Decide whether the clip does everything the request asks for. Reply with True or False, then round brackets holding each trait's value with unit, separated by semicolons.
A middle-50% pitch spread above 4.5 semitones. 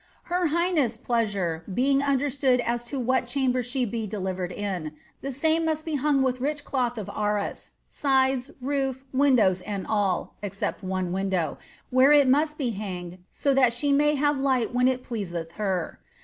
True (5.5 semitones)